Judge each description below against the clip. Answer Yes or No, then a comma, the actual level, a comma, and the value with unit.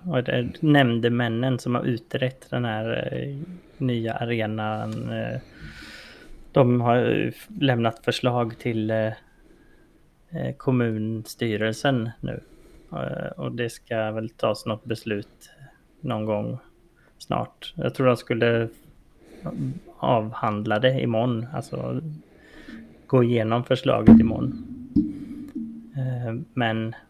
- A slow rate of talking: Yes, slow, 85 wpm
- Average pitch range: Yes, average, 3.0 semitones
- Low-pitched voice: Yes, low, 120 Hz